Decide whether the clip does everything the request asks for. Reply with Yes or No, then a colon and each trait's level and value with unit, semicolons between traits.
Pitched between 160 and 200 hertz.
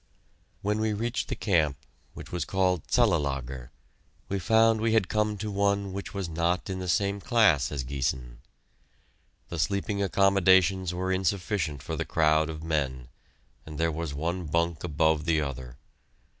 No: very low, 85 Hz